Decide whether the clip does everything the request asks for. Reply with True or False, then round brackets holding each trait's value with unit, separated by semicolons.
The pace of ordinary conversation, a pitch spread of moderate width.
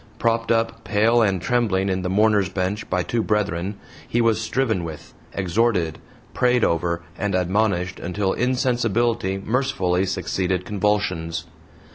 False (130 wpm; 3.8 semitones)